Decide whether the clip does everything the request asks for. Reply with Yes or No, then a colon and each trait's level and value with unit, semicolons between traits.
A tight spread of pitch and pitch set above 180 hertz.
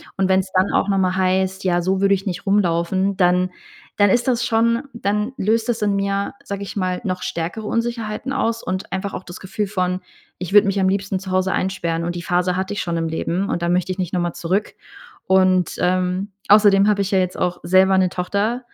Yes: narrow, 1.9 semitones; high, 190 Hz